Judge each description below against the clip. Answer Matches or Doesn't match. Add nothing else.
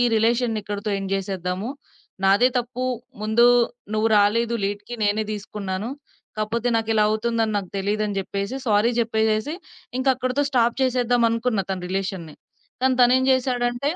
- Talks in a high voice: Matches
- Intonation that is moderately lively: Matches